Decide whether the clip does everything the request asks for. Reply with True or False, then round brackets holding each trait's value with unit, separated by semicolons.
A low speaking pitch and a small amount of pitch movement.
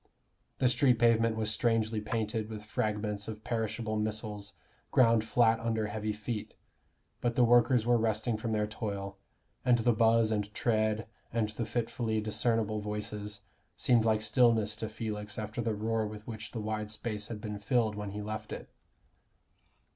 True (110 Hz; 1.4 semitones)